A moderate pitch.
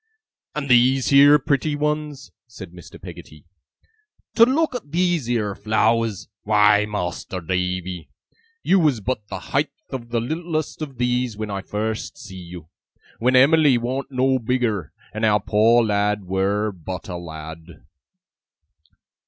No: low, 115 Hz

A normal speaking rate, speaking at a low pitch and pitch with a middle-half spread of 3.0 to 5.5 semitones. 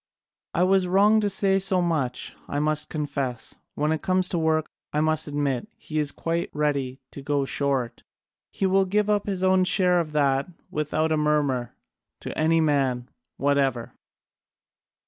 No: average, 165 wpm; medium, 155 Hz; average, 4.5 semitones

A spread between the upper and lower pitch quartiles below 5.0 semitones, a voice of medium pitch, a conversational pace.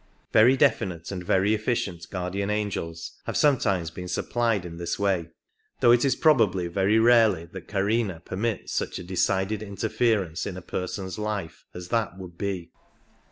No: average, 3.6 semitones; low, 100 Hz; average, 165 wpm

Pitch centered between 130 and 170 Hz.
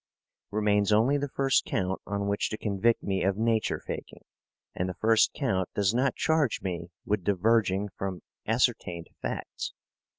No: low, 105 Hz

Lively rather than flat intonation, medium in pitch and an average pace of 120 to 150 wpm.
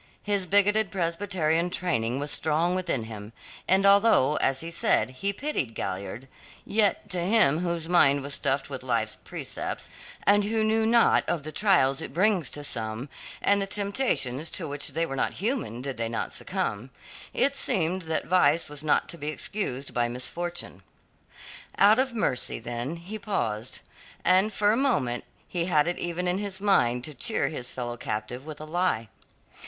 No: wide, 7.3 semitones; medium, 165 Hz; average, 175 wpm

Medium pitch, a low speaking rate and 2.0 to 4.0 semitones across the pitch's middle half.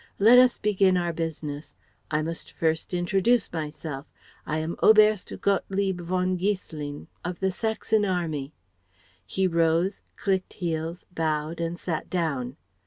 Yes: medium, 175 Hz; slow, 130 wpm; average, 3.3 semitones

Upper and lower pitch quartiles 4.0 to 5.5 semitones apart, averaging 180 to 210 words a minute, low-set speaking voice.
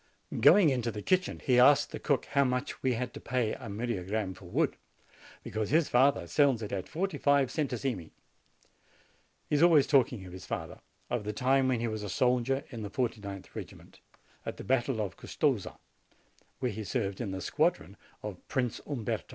Yes: average, 4.3 semitones; average, 185 wpm; low, 125 Hz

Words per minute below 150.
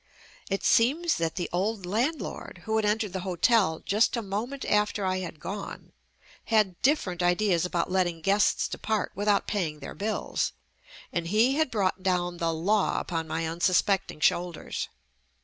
No: average, 165 wpm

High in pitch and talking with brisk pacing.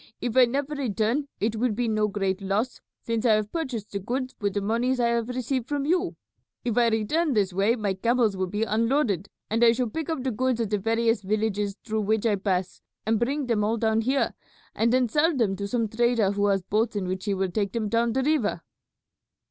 Yes: high, 225 Hz; fast, 230 wpm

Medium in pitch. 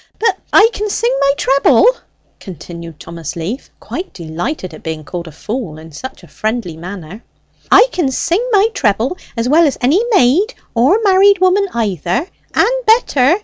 No: very high, 250 Hz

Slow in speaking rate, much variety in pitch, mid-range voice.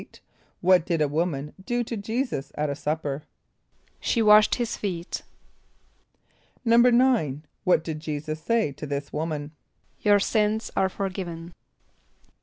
Yes: slow, 130 wpm; wide, 6.2 semitones; medium, 175 Hz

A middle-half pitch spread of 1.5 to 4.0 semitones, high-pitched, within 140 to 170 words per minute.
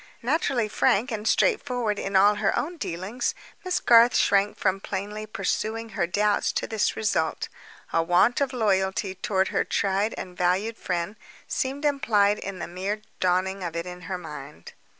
Yes: average, 3.5 semitones; high, 205 Hz; average, 165 wpm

